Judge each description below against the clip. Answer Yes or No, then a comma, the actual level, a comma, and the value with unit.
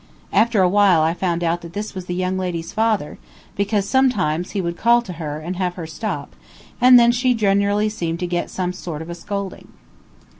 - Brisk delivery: Yes, fast, 210 wpm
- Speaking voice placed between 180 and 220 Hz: Yes, medium, 185 Hz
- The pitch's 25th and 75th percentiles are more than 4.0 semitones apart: No, average, 3.6 semitones